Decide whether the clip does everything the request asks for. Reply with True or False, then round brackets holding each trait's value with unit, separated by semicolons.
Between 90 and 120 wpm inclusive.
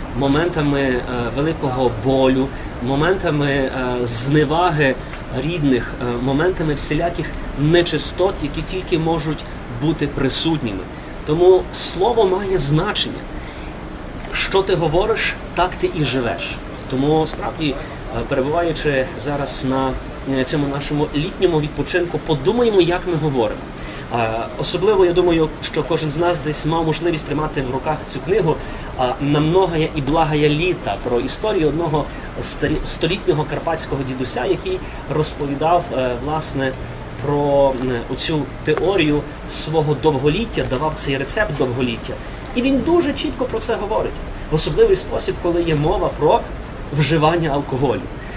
True (115 wpm)